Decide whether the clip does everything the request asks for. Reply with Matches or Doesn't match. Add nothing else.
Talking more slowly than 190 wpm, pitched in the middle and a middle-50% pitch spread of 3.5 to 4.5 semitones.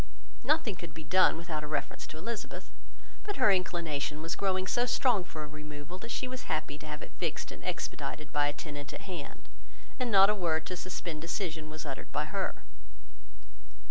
Doesn't match